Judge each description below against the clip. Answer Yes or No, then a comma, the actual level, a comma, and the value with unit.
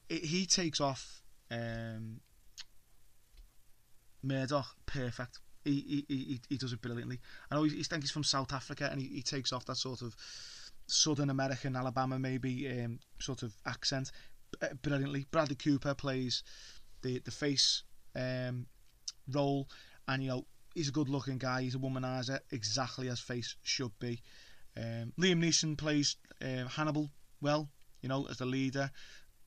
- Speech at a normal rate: Yes, average, 150 wpm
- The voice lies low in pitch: Yes, low, 130 Hz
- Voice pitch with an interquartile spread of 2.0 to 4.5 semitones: Yes, narrow, 2.4 semitones